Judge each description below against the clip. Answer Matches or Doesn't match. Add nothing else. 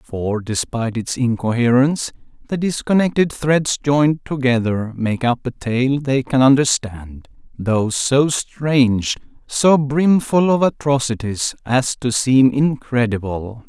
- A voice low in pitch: Matches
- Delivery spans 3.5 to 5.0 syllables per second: Matches